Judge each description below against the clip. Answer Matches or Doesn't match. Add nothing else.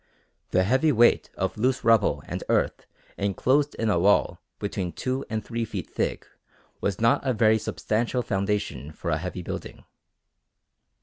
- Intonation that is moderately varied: Matches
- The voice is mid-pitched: Doesn't match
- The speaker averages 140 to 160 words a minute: Matches